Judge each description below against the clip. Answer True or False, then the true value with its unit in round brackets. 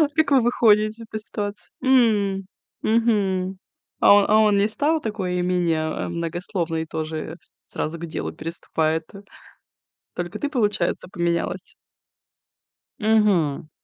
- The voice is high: True (195 Hz)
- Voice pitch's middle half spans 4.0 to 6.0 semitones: True (4.3 semitones)